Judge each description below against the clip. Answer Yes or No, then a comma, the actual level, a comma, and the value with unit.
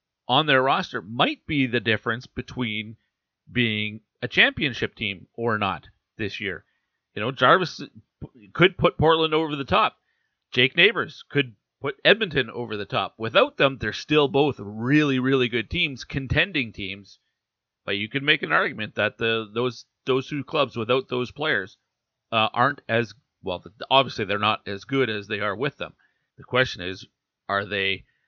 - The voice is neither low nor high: No, low, 120 Hz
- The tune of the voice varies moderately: Yes, average, 4.5 semitones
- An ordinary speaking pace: Yes, average, 165 wpm